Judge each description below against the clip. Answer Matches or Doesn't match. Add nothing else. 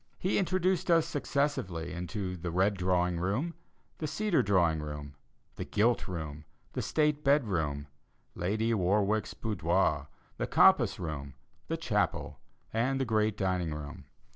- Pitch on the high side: Doesn't match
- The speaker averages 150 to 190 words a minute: Doesn't match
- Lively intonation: Matches